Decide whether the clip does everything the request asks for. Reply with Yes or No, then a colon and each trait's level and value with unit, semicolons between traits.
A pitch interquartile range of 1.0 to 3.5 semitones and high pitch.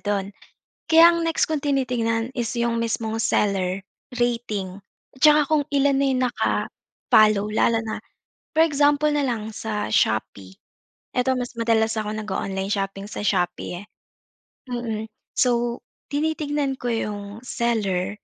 No: average, 4.5 semitones; high, 230 Hz